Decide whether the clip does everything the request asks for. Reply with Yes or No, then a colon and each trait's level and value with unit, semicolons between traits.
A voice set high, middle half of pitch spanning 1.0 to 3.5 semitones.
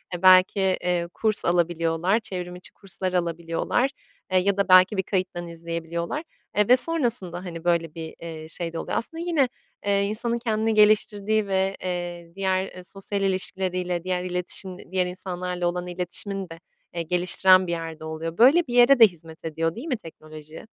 No: medium, 180 Hz; average, 2.9 semitones